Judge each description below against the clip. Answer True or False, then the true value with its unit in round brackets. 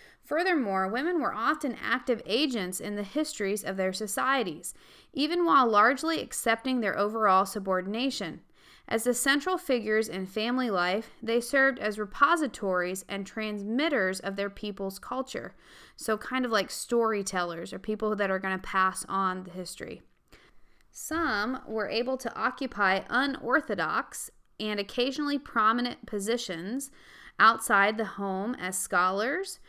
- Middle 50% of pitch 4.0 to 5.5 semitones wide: True (4.8 semitones)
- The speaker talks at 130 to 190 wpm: True (135 wpm)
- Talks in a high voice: True (220 Hz)